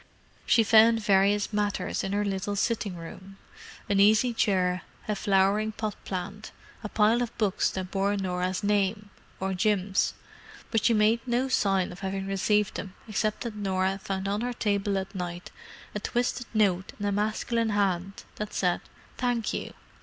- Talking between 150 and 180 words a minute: Yes, average, 160 wpm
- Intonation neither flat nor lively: No, narrow, 2.0 semitones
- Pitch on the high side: Yes, high, 205 Hz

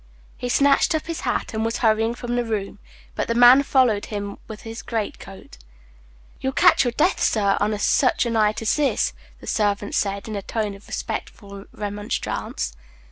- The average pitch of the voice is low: No, high, 220 Hz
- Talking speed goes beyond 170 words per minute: Yes, average, 185 wpm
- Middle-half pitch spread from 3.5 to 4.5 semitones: No, average, 3.0 semitones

